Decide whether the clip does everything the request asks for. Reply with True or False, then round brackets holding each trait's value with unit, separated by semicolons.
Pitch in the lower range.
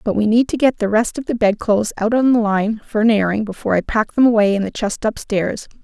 False (220 Hz)